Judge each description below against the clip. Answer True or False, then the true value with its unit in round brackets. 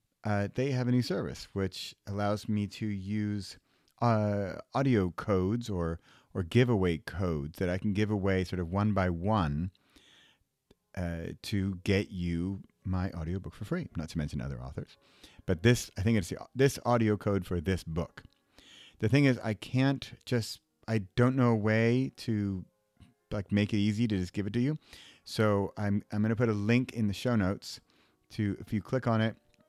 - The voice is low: True (105 Hz)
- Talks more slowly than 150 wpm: False (190 wpm)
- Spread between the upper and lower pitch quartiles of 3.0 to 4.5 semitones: True (3.5 semitones)